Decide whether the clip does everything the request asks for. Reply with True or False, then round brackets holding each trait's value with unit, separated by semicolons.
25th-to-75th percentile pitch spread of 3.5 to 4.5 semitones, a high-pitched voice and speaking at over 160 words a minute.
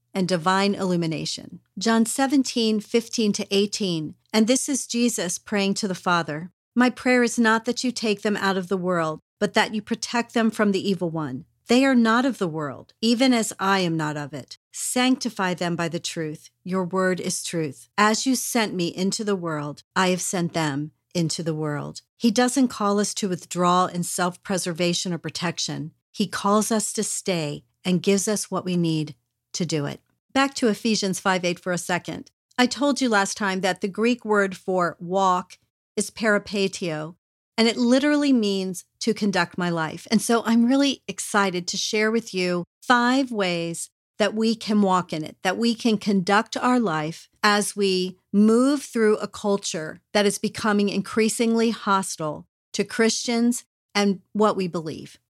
True (4.2 semitones; 200 Hz; 180 wpm)